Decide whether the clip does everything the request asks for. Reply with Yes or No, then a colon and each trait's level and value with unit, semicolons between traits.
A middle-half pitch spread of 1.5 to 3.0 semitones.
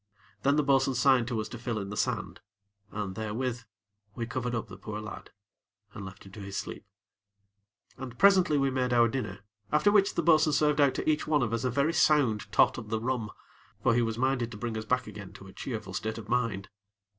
No: average, 4.0 semitones